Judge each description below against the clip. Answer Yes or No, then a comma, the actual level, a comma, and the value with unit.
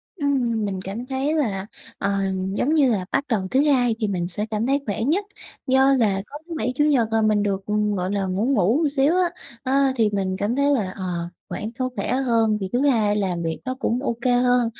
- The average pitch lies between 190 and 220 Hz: No, high, 230 Hz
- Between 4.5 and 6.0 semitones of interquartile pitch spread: Yes, average, 4.9 semitones